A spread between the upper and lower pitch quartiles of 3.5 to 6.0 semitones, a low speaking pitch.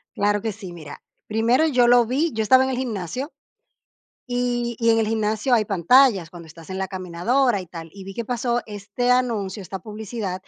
No: average, 4.3 semitones; high, 220 Hz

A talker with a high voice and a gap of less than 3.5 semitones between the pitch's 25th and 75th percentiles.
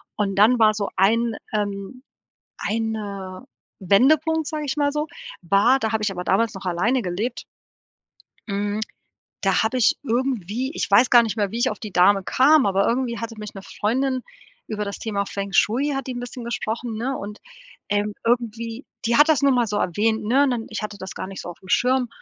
No: high, 225 Hz; average, 3.9 semitones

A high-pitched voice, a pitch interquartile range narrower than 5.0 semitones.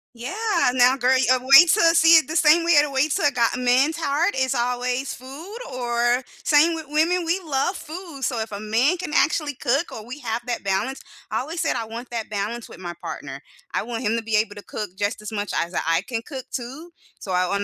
No: very high, 255 Hz; average, 5.3 semitones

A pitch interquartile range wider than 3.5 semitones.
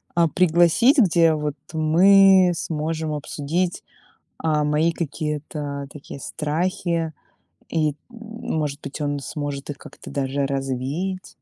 No: average, 3.1 semitones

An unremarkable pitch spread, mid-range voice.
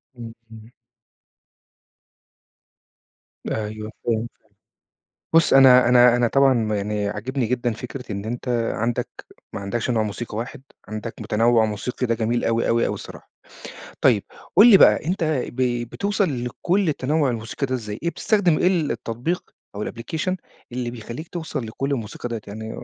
No: average, 3.6 semitones; low, 120 Hz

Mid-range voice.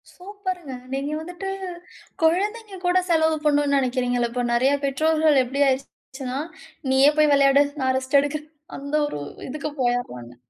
No: very high, 280 Hz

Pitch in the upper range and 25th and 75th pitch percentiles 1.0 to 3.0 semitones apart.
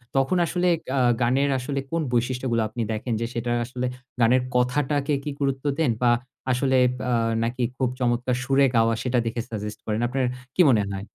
No: low, 125 Hz; narrow, 2.4 semitones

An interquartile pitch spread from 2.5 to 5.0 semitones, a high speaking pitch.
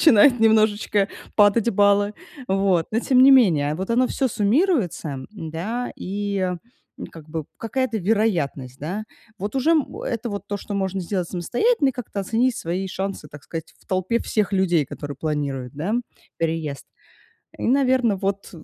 No: wide, 5.4 semitones; high, 200 Hz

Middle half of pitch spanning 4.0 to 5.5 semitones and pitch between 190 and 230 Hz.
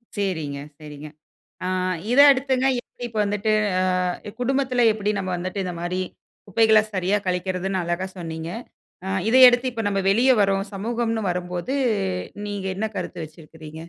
Yes: average, 4.4 semitones; high, 195 Hz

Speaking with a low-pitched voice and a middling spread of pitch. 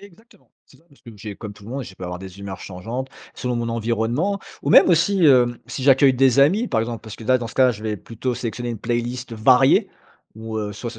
Yes: low, 120 Hz; average, 3.3 semitones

